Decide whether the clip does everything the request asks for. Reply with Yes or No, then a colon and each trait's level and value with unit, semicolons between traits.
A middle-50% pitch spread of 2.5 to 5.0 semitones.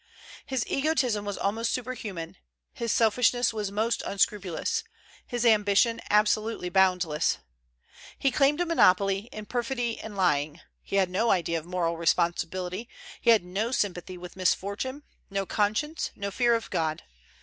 Yes: average, 4.4 semitones